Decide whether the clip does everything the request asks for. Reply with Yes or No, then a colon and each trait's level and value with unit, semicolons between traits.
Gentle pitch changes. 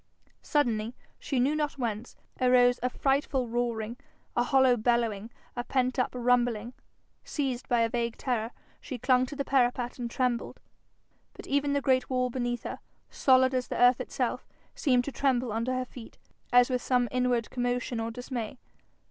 Yes: narrow, 1.3 semitones